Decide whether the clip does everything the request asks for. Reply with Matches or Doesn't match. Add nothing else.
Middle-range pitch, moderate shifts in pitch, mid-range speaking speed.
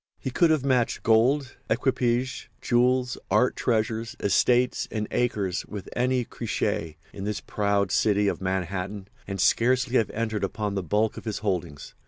Doesn't match